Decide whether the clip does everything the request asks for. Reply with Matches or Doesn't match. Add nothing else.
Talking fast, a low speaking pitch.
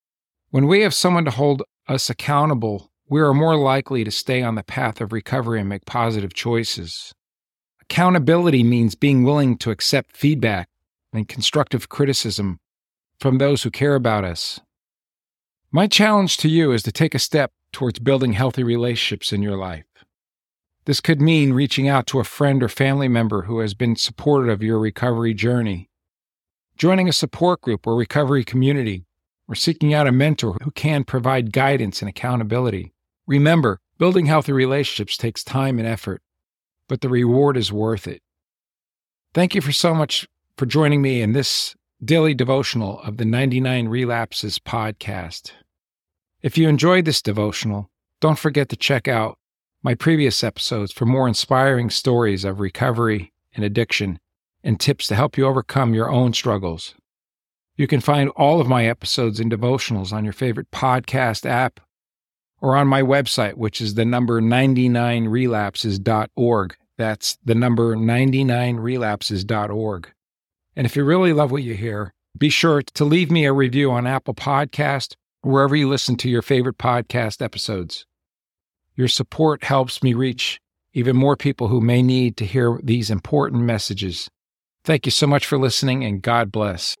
Doesn't match